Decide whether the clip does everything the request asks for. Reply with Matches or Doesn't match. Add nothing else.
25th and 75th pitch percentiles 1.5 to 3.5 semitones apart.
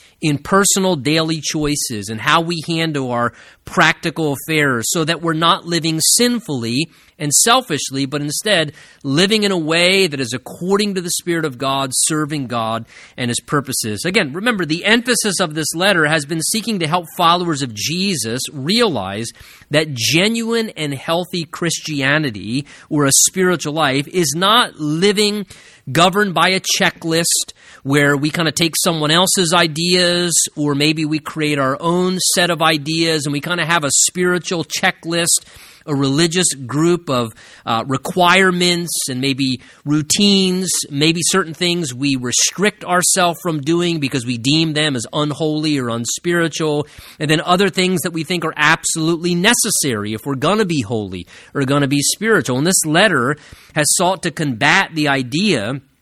Doesn't match